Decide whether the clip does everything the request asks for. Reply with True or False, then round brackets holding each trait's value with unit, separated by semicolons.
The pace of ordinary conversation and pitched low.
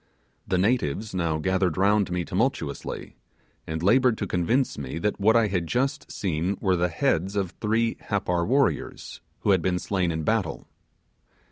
True (160 wpm; 95 Hz)